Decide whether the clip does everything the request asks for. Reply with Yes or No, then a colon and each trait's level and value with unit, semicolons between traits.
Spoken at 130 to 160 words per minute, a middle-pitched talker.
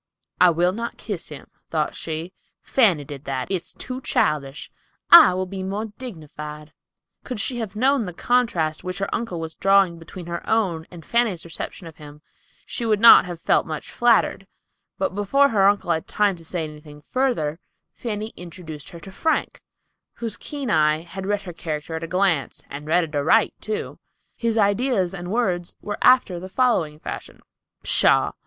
No: average, 175 wpm; medium, 180 Hz